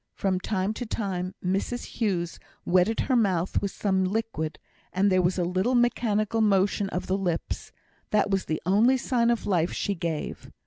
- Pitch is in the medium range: No, high, 195 Hz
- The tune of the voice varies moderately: Yes, average, 3.3 semitones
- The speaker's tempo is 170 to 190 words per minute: Yes, average, 175 wpm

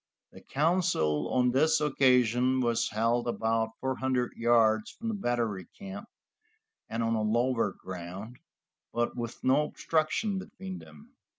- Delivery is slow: Yes, slow, 130 wpm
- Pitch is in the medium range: No, low, 125 Hz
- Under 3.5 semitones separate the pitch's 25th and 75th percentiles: No, average, 5.1 semitones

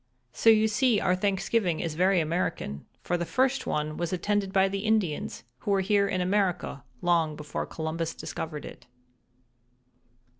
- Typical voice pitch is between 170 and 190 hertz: Yes, medium, 185 Hz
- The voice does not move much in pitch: No, average, 3.9 semitones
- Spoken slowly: No, average, 155 wpm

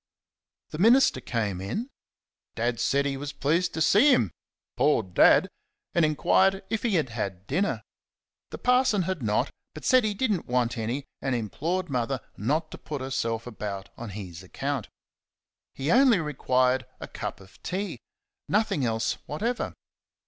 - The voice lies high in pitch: No, medium, 140 Hz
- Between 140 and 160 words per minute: Yes, average, 155 wpm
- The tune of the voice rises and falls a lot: Yes, wide, 8.4 semitones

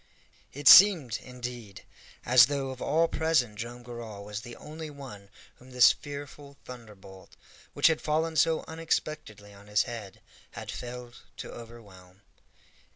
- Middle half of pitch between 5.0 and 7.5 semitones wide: Yes, average, 5.3 semitones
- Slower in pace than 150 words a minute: Yes, average, 140 wpm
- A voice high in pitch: No, low, 125 Hz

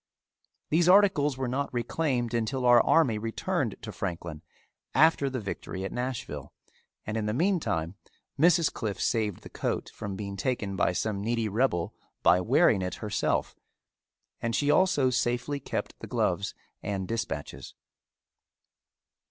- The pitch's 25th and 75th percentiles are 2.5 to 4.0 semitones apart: No, average, 5.3 semitones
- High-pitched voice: No, low, 120 Hz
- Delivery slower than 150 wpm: Yes, average, 140 wpm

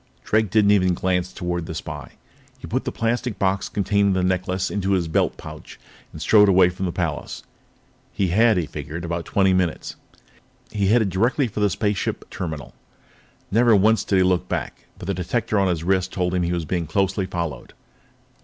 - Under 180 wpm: No, average, 190 wpm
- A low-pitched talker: Yes, very low, 95 Hz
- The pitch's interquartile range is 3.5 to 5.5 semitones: No, narrow, 2.6 semitones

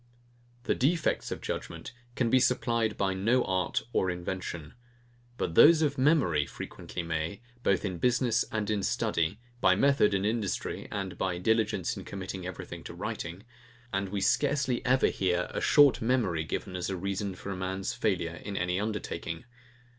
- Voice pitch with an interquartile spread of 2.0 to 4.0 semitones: No, average, 4.5 semitones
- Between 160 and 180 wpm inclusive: Yes, average, 165 wpm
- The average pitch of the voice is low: Yes, low, 100 Hz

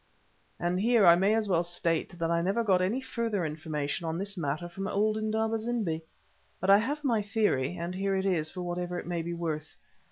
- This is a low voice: No, medium, 185 Hz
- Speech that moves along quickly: Yes, fast, 215 wpm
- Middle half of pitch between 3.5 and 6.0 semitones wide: Yes, average, 4.1 semitones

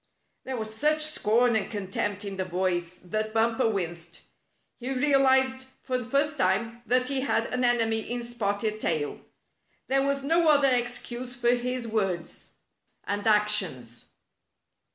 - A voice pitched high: Yes, high, 235 Hz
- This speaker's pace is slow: No, average, 150 wpm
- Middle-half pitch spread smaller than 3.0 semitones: No, average, 4.3 semitones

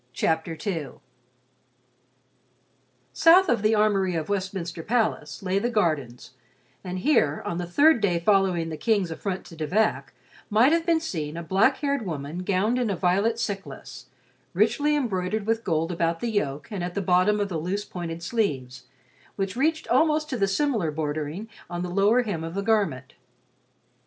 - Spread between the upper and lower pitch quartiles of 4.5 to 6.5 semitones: Yes, average, 5.1 semitones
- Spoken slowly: No, average, 170 wpm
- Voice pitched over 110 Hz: Yes, high, 190 Hz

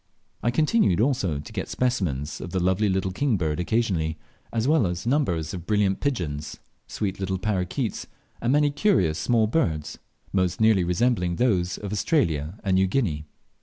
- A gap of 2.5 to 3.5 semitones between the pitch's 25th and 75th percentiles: No, wide, 5.5 semitones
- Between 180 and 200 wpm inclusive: No, average, 165 wpm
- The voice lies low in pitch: Yes, very low, 95 Hz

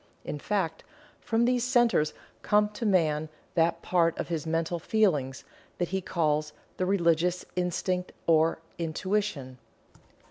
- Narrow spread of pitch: No, average, 4.0 semitones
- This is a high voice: No, medium, 175 Hz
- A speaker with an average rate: No, slow, 130 wpm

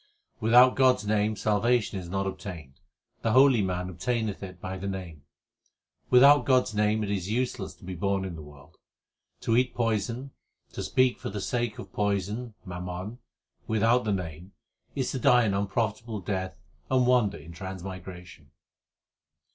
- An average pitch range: Yes, average, 4.3 semitones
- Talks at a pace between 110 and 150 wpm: No, average, 165 wpm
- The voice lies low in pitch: Yes, low, 105 Hz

